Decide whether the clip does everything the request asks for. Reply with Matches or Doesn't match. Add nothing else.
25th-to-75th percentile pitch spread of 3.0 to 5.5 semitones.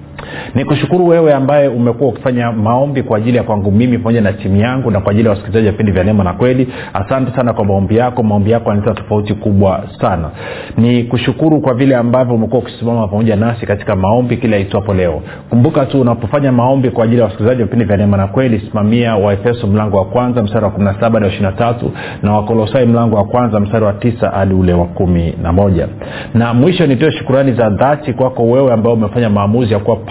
Matches